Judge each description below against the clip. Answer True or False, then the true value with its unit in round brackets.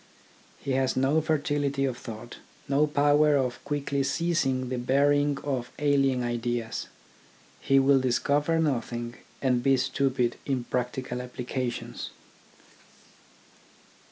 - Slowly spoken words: True (115 wpm)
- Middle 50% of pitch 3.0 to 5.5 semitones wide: False (2.5 semitones)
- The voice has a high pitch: False (135 Hz)